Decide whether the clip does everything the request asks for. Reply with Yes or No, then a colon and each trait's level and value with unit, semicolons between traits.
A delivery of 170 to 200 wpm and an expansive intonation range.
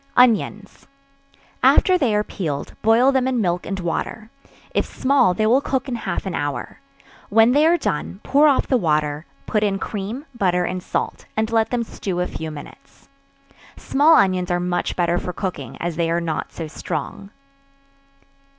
Yes: average, 175 wpm; wide, 5.8 semitones